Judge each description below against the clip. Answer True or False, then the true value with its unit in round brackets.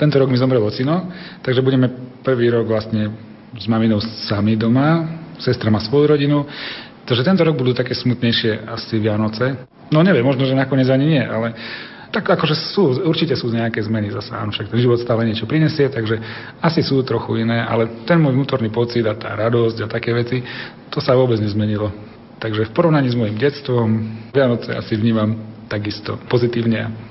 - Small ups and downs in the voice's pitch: False (3.3 semitones)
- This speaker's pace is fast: True (175 wpm)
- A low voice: True (120 Hz)